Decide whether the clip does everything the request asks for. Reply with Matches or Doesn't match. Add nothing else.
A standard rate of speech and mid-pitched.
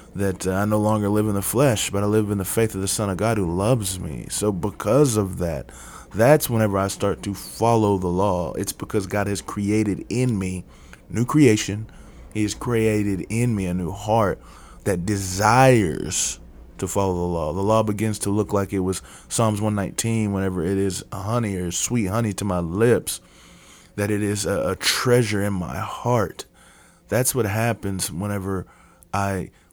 Doesn't match